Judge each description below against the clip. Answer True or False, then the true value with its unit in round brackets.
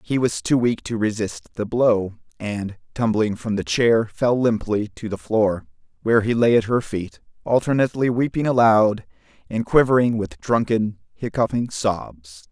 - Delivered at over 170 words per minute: False (160 wpm)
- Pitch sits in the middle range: False (110 Hz)